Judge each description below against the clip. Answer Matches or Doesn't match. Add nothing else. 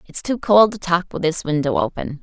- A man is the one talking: Doesn't match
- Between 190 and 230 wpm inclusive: Doesn't match